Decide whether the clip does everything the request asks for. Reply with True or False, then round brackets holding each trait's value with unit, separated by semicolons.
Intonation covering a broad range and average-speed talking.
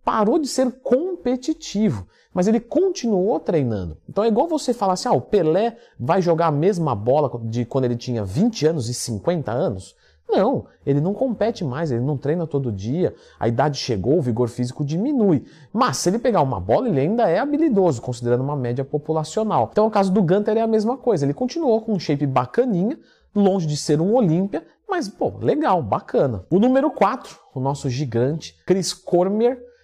False (8.7 semitones; 190 wpm)